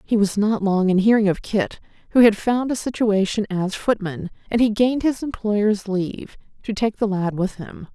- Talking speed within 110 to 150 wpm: No, fast, 205 wpm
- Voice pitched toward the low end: No, high, 210 Hz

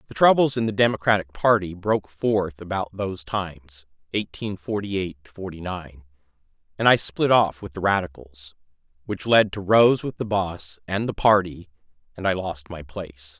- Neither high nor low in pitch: No, very low, 95 Hz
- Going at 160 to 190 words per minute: Yes, average, 165 wpm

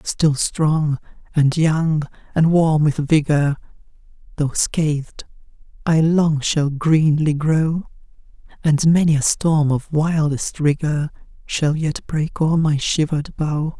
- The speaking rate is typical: No, slow, 125 wpm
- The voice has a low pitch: No, medium, 155 Hz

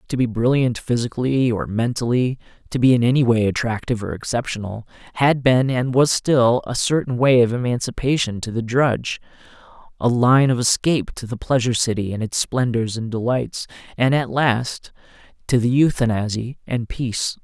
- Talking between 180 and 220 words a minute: No, average, 165 wpm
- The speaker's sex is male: Yes, male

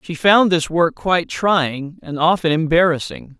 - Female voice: No, male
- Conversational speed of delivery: Yes, average, 160 wpm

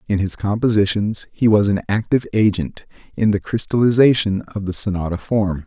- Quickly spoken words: No, average, 160 wpm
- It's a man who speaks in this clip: Yes, male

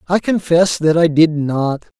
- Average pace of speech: Yes, average, 180 wpm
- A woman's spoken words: No, male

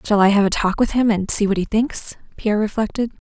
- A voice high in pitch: Yes, high, 210 Hz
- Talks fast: Yes, fast, 255 wpm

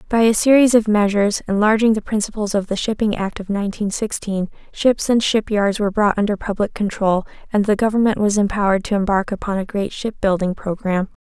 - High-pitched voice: Yes, high, 205 Hz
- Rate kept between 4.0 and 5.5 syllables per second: No, 5.9 syllables/s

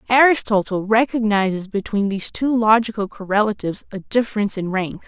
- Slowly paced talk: Yes, slow, 130 wpm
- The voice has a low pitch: No, high, 210 Hz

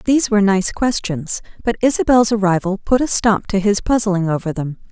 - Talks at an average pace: Yes, average, 185 wpm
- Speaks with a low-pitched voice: No, high, 205 Hz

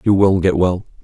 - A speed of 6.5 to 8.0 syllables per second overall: No, 5.1 syllables/s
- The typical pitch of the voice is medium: No, very low, 95 Hz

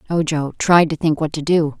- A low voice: No, medium, 155 Hz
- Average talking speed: No, fast, 235 wpm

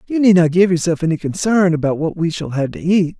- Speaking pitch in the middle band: Yes, medium, 170 Hz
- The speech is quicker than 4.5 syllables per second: Yes, 5.9 syllables/s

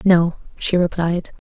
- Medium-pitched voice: Yes, medium, 175 Hz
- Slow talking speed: Yes, slow, 120 wpm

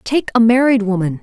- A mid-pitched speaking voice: No, high, 225 Hz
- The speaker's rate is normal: Yes, average, 195 wpm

